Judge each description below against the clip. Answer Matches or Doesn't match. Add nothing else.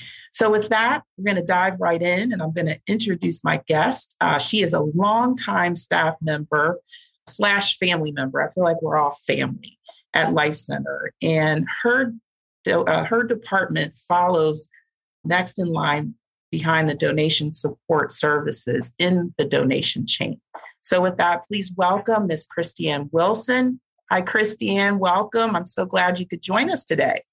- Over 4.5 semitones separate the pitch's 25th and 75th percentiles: Matches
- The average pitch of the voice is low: Doesn't match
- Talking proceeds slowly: Doesn't match